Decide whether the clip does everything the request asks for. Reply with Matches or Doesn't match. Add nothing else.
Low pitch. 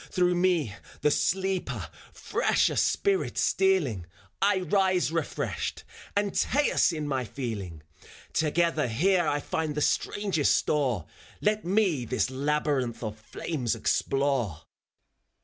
Doesn't match